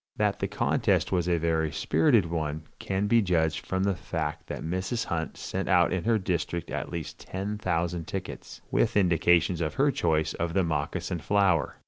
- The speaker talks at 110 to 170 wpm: No, average, 180 wpm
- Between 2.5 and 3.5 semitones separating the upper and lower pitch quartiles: Yes, average, 2.8 semitones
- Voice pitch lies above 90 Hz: No, very low, 85 Hz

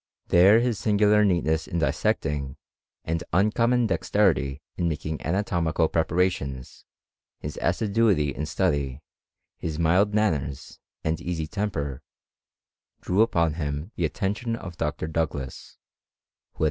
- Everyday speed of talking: No, slow, 125 wpm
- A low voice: Yes, very low, 85 Hz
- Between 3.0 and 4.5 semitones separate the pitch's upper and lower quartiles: No, average, 5.3 semitones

